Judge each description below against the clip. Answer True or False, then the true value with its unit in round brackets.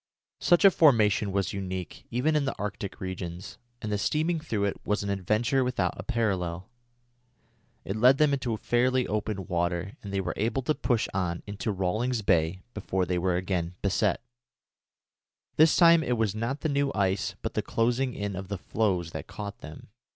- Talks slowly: False (180 wpm)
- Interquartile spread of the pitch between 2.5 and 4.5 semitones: False (4.9 semitones)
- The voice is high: False (105 Hz)